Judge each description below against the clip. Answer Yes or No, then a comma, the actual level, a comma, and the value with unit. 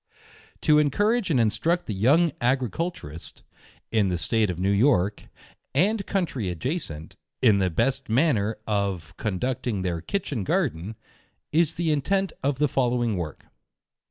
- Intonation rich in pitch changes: Yes, wide, 7.6 semitones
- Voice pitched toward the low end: Yes, low, 120 Hz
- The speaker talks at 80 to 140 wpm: Yes, slow, 135 wpm